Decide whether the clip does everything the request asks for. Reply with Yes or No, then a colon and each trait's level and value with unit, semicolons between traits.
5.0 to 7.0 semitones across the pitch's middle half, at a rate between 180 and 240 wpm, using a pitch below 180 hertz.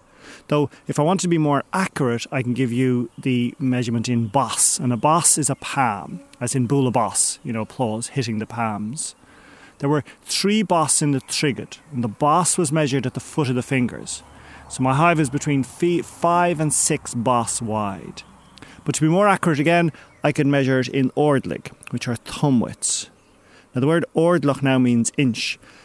No: average, 4.0 semitones; average, 195 wpm; low, 135 Hz